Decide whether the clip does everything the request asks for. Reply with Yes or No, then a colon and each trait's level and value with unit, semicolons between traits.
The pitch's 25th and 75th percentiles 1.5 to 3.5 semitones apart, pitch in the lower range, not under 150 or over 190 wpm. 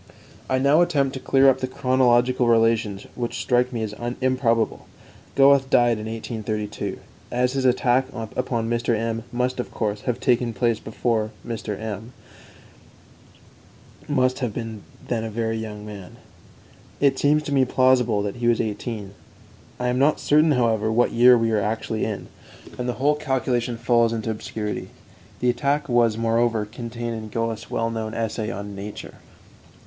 Yes: narrow, 2.5 semitones; low, 120 Hz; average, 160 wpm